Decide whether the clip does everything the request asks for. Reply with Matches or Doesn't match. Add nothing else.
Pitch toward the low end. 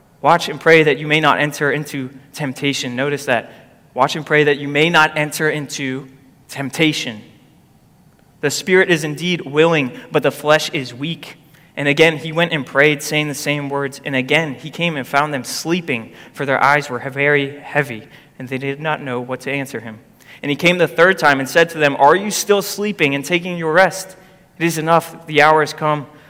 Doesn't match